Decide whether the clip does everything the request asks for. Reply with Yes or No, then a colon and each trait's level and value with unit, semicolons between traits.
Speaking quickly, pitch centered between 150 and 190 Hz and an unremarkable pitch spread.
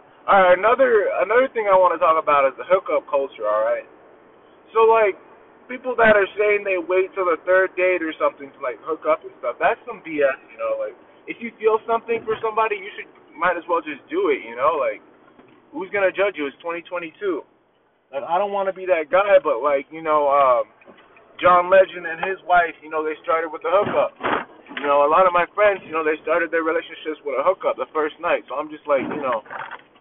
No: fast, 220 wpm; medium, 185 Hz; wide, 5.8 semitones